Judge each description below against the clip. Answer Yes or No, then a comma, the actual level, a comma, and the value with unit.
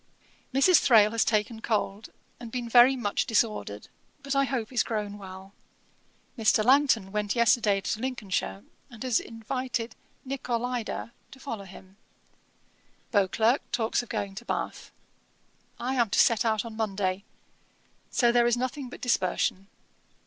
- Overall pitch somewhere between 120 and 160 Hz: No, high, 225 Hz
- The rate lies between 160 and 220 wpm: No, average, 140 wpm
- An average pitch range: Yes, average, 3.3 semitones